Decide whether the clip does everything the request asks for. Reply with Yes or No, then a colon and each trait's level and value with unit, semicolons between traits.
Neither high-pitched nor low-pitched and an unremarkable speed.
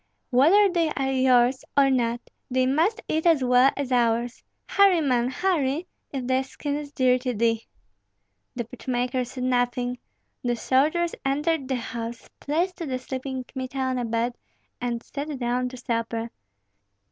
No: very high, 255 Hz; average, 160 wpm